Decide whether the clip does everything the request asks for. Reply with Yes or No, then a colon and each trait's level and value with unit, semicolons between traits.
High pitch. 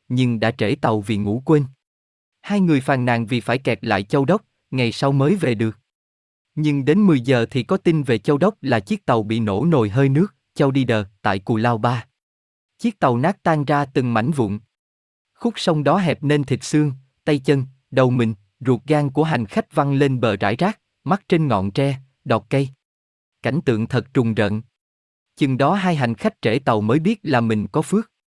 No: low, 135 Hz